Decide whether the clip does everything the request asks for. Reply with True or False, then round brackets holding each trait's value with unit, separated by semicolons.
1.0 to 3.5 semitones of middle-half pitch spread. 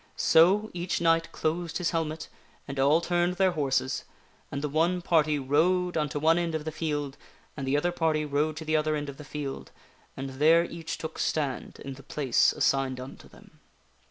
True (2.8 semitones)